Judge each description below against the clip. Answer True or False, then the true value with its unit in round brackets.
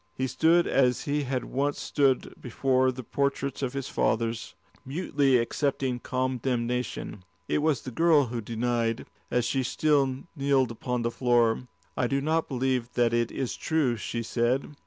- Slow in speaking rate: False (155 wpm)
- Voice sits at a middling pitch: False (130 Hz)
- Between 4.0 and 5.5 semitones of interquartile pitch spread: False (2.5 semitones)